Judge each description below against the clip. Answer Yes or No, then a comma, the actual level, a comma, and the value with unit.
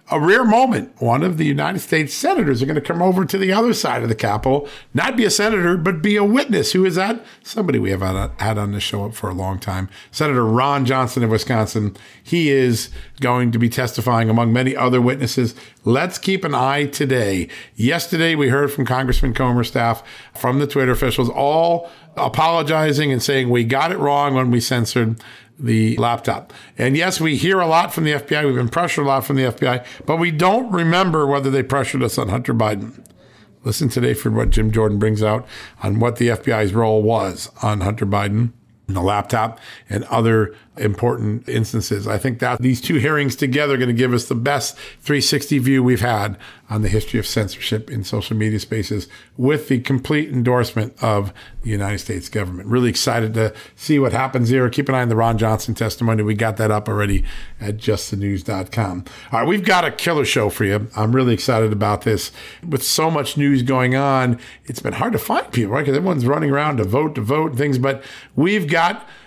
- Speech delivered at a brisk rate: Yes, fast, 210 wpm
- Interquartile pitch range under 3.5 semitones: No, average, 4.5 semitones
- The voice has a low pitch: Yes, low, 125 Hz